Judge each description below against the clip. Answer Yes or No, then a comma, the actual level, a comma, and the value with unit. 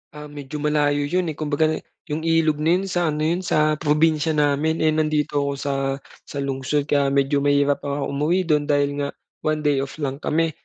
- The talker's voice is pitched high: No, medium, 150 Hz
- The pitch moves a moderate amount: No, narrow, 1.6 semitones